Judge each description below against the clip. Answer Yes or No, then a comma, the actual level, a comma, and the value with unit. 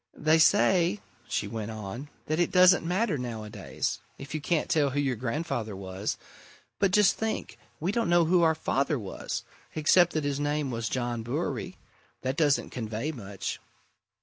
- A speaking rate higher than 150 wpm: Yes, average, 165 wpm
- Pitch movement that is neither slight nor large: No, wide, 6.8 semitones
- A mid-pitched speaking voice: Yes, medium, 145 Hz